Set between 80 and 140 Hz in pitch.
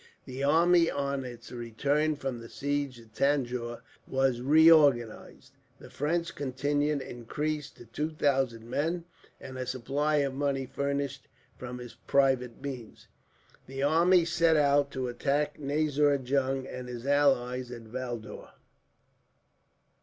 Yes: low, 135 Hz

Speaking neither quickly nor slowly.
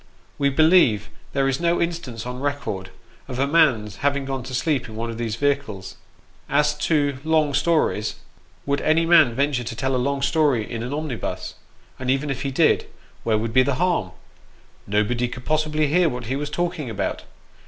Yes: average, 185 wpm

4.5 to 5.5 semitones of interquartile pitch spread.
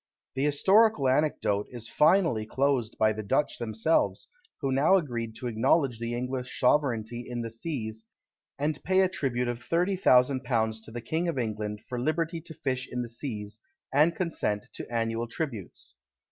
Yes: average, 4.9 semitones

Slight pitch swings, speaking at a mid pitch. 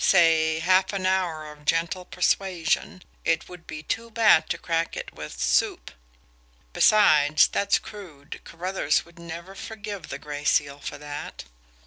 No: average, 3.6 semitones; medium, 170 Hz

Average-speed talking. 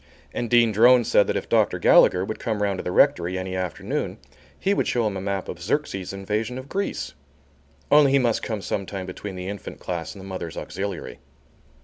No: fast, 210 wpm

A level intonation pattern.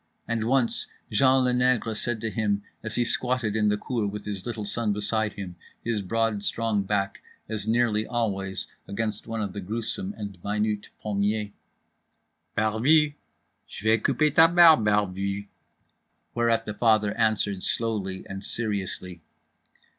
Yes: narrow, 2.3 semitones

